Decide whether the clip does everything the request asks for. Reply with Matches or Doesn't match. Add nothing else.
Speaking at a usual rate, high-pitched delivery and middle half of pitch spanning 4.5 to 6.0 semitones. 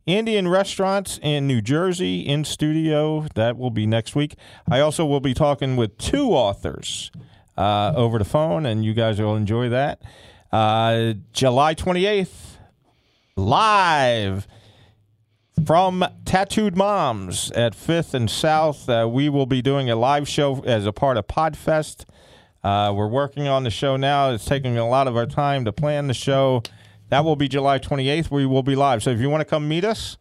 Doesn't match